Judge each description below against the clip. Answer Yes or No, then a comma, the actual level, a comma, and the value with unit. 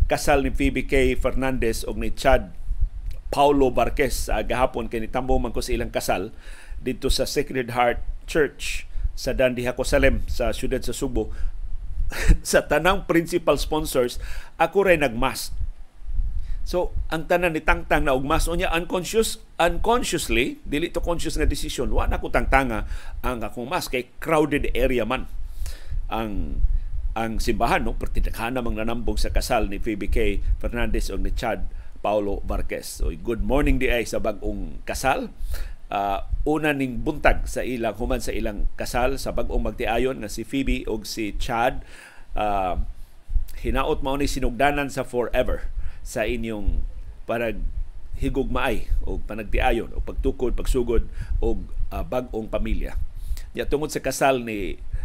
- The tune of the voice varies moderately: No, wide, 6.0 semitones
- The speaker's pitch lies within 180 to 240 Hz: No, low, 120 Hz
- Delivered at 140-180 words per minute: Yes, average, 145 wpm